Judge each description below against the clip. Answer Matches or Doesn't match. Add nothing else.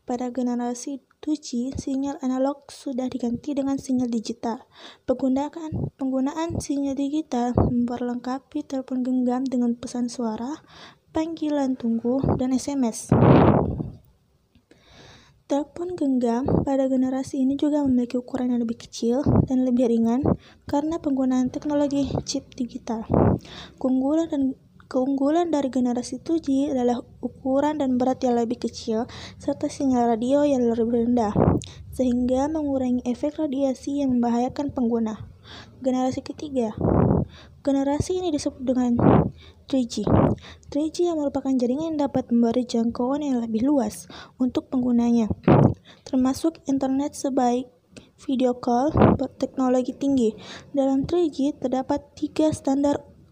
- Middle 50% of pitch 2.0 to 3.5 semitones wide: Matches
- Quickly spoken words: Doesn't match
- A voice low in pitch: Doesn't match